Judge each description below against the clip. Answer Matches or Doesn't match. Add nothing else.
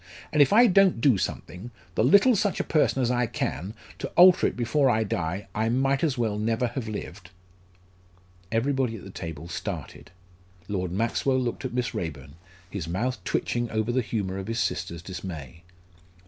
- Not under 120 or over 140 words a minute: Doesn't match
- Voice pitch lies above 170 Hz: Doesn't match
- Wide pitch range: Matches